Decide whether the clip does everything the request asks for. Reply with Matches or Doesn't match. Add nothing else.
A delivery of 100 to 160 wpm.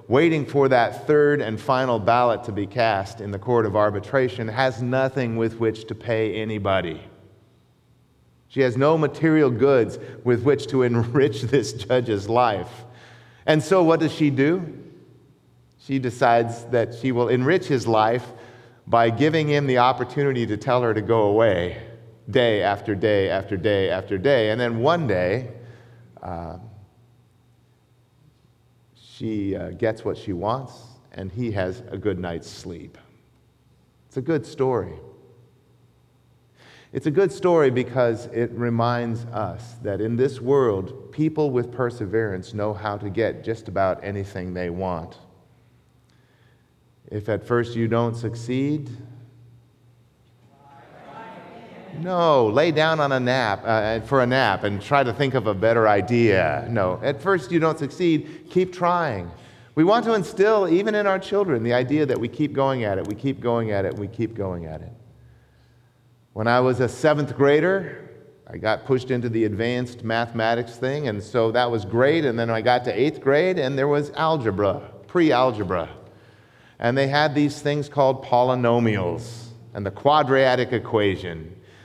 Matches